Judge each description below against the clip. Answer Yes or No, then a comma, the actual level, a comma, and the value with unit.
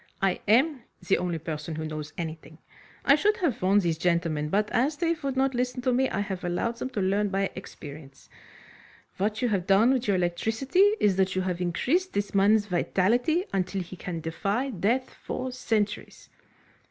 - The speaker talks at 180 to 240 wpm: Yes, average, 185 wpm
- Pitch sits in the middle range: No, high, 200 Hz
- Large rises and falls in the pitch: Yes, wide, 6.1 semitones